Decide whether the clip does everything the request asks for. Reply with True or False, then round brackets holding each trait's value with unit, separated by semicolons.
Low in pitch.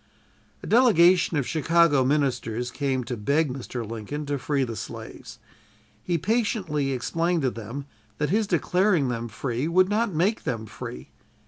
False (145 Hz)